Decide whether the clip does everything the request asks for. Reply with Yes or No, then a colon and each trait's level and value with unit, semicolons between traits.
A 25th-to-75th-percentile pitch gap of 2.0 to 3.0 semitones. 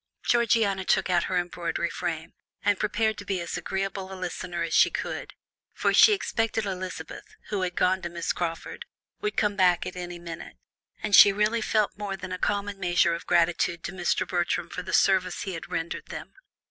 Yes: average, 2.7 semitones